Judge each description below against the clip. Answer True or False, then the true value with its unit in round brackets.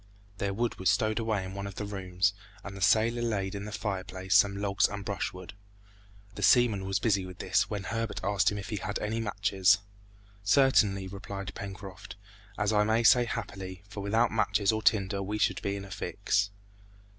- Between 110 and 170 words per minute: False (190 wpm)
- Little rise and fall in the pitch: True (1.9 semitones)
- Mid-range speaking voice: False (100 Hz)